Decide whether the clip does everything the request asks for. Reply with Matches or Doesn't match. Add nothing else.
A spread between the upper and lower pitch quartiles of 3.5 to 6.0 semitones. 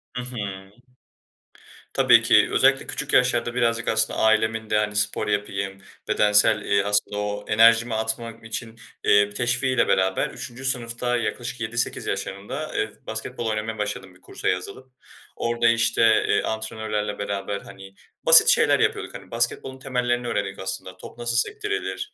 Doesn't match